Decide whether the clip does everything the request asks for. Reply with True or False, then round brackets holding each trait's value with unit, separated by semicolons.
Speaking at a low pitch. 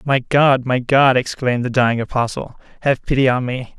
True (130 Hz)